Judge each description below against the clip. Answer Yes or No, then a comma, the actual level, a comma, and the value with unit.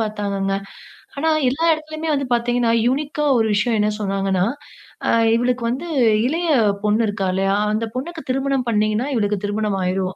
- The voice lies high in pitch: Yes, high, 230 Hz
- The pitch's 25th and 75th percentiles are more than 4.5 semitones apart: Yes, average, 4.9 semitones